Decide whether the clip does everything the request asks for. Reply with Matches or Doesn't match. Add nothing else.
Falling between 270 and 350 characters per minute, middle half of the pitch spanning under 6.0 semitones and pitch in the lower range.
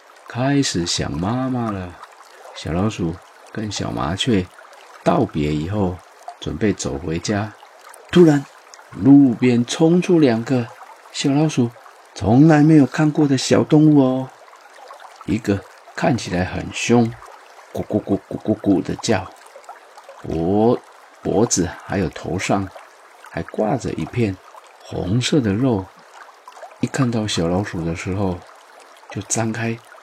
Doesn't match